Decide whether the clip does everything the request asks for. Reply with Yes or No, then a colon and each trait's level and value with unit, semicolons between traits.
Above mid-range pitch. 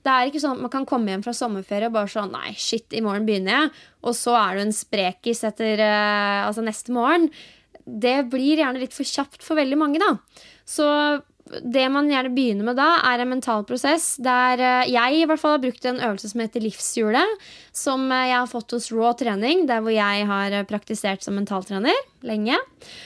Yes: high, 245 Hz